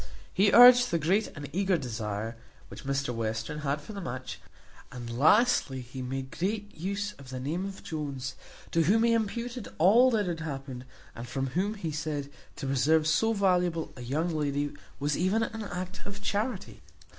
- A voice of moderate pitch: Yes, medium, 160 Hz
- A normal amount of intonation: No, wide, 6.9 semitones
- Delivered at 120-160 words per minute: No, average, 180 wpm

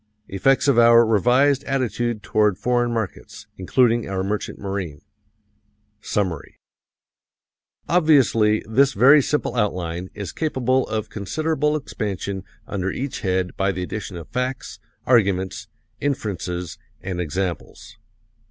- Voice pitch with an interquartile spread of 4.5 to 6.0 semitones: Yes, average, 5.3 semitones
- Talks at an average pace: No, slow, 115 wpm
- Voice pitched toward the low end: Yes, low, 110 Hz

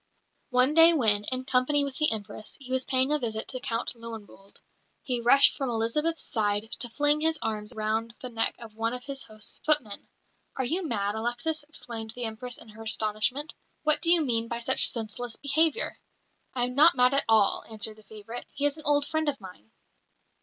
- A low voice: No, high, 245 Hz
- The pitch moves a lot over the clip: No, average, 4.6 semitones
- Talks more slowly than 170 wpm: No, average, 200 wpm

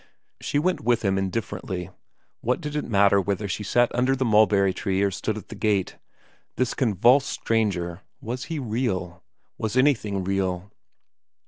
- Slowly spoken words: No, average, 155 wpm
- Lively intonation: No, average, 4.3 semitones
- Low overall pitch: Yes, low, 105 Hz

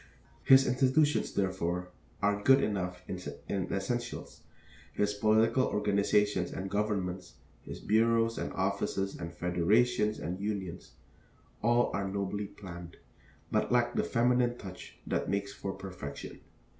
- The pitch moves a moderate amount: Yes, average, 3.7 semitones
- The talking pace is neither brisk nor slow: No, slow, 120 wpm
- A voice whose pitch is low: Yes, low, 100 Hz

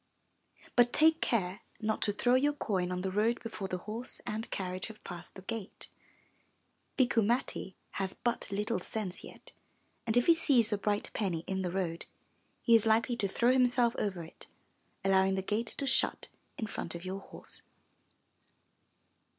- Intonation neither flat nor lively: Yes, average, 3.9 semitones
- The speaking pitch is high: Yes, high, 210 Hz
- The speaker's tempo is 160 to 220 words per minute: Yes, average, 170 wpm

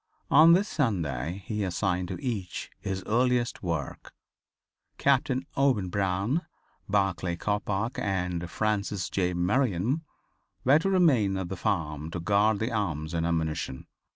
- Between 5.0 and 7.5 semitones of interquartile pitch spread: Yes, wide, 5.4 semitones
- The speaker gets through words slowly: Yes, slow, 130 wpm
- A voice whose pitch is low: Yes, low, 100 Hz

